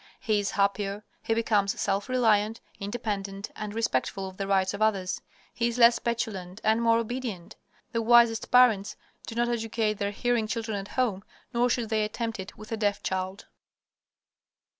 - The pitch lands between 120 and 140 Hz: No, high, 215 Hz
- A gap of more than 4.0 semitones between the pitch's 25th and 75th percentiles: No, average, 2.7 semitones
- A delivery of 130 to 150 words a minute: No, average, 170 wpm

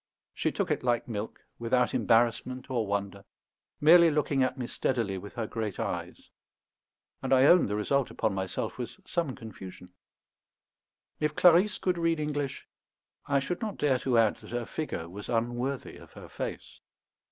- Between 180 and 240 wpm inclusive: No, average, 165 wpm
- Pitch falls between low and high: No, low, 125 Hz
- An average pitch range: Yes, average, 4.8 semitones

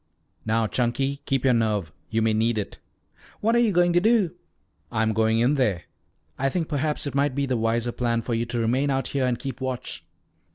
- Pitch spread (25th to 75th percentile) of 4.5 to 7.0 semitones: No, average, 3.8 semitones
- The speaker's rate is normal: No, fast, 210 wpm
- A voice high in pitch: No, low, 125 Hz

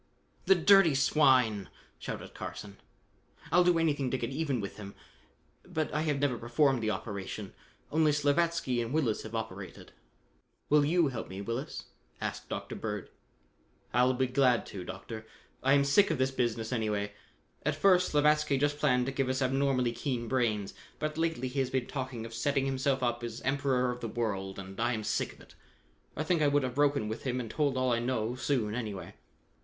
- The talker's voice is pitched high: No, low, 130 Hz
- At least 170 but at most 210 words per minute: Yes, average, 190 wpm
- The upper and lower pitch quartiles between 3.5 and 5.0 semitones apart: Yes, average, 3.9 semitones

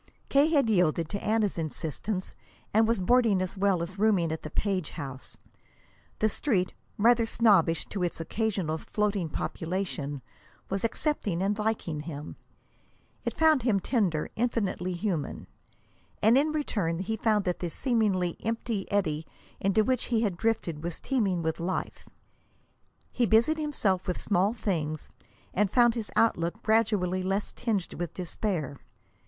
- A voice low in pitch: No, high, 195 Hz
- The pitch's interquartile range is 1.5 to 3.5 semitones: No, average, 4.6 semitones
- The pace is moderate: Yes, average, 145 wpm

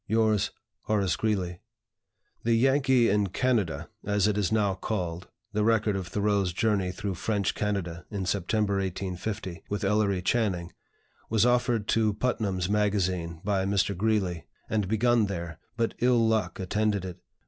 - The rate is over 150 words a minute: No, average, 145 wpm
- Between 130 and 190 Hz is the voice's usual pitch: No, low, 100 Hz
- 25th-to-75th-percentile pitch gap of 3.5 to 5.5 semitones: No, average, 2.8 semitones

